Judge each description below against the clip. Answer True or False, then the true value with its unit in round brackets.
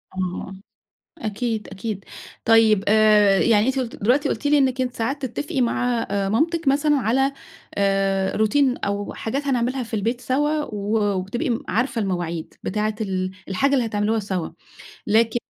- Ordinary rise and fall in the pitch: True (4.4 semitones)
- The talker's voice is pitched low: False (225 Hz)